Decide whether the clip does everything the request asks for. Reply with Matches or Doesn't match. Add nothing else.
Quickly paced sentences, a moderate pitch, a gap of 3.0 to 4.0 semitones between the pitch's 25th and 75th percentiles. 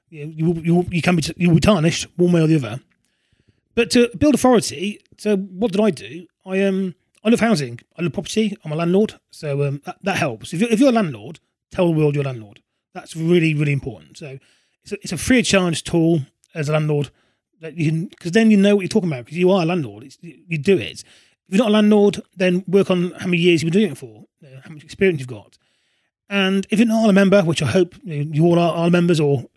Doesn't match